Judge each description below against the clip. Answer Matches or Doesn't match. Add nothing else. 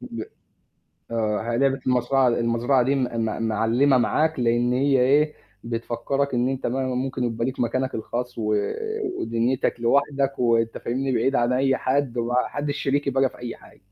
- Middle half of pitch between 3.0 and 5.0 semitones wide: Doesn't match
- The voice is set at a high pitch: Doesn't match